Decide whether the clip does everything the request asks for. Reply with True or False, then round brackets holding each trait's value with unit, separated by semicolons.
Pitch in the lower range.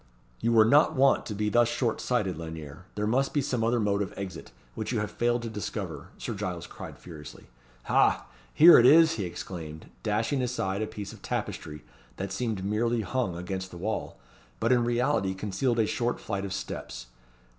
True (105 Hz)